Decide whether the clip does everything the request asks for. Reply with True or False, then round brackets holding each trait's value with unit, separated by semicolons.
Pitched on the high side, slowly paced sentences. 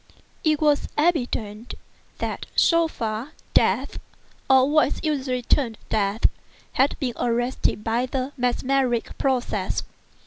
True (255 Hz; 115 wpm)